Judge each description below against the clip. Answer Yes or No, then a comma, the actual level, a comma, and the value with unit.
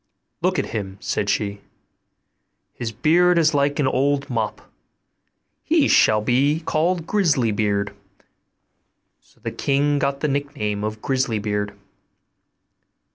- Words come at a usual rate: No, slow, 125 wpm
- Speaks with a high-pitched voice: No, low, 130 Hz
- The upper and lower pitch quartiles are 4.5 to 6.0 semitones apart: Yes, wide, 5.4 semitones